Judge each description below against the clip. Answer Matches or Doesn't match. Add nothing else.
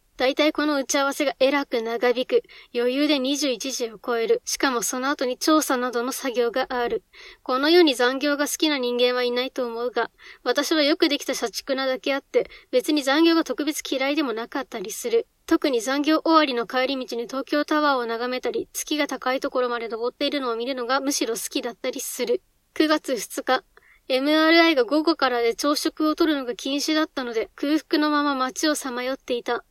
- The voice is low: Doesn't match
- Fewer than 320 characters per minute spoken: Doesn't match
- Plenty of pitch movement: Doesn't match